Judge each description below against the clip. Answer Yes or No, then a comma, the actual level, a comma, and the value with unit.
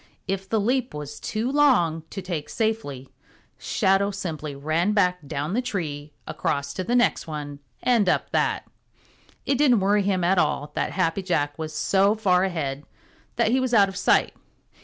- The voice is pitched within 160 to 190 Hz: Yes, medium, 185 Hz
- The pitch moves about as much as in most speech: No, wide, 5.8 semitones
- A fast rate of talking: No, average, 175 wpm